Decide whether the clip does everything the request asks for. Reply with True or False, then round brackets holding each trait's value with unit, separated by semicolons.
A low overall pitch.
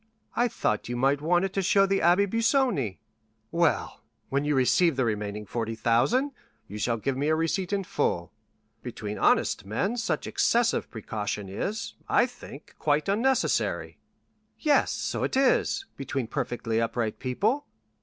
False (150 Hz)